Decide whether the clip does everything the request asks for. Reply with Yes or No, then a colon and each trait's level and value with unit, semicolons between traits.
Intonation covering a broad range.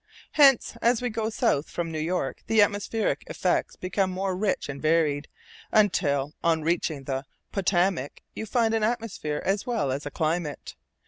Yes: wide, 6.1 semitones